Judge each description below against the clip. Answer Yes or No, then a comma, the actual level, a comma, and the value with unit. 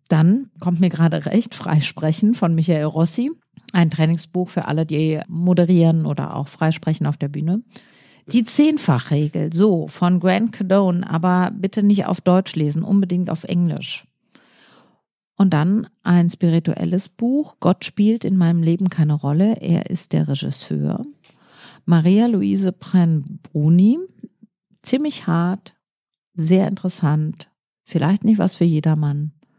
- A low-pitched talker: No, medium, 180 Hz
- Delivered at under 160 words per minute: Yes, average, 130 wpm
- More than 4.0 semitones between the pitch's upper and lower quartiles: No, average, 3.6 semitones